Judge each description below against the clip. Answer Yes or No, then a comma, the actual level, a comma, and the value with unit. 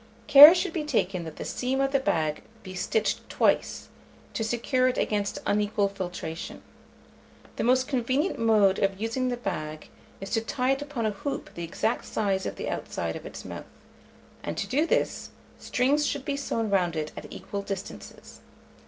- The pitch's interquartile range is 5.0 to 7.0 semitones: Yes, wide, 5.5 semitones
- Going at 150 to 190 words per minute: Yes, average, 180 wpm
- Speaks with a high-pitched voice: Yes, high, 225 Hz